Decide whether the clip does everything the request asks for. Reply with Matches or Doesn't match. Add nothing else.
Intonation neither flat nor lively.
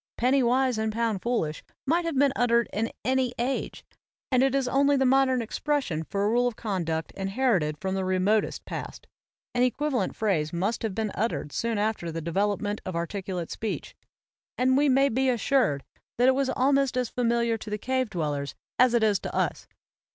Matches